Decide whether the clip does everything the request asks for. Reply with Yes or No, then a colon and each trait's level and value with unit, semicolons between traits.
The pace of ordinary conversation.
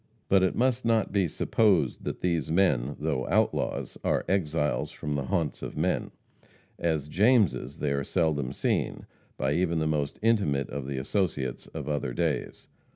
Yes: average, 160 wpm